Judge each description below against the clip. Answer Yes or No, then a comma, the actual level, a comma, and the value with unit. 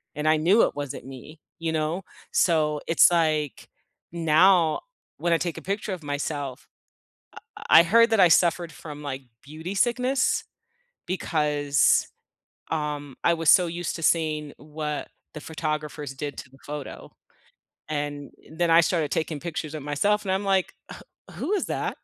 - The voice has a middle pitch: Yes, medium, 155 Hz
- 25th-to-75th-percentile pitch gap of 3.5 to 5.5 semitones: No, average, 2.8 semitones